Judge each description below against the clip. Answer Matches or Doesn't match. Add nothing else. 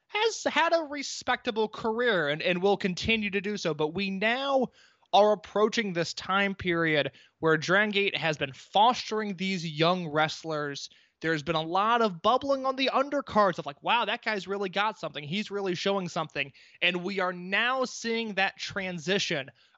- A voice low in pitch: Doesn't match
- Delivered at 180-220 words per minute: Doesn't match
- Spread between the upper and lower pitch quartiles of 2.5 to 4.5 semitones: Doesn't match